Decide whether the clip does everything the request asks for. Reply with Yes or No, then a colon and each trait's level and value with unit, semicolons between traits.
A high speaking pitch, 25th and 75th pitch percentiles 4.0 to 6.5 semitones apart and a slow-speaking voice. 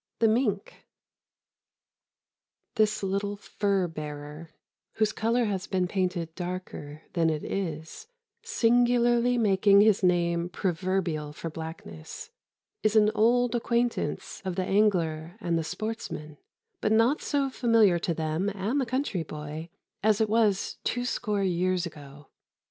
Yes: high, 195 Hz; average, 5.1 semitones; slow, 130 wpm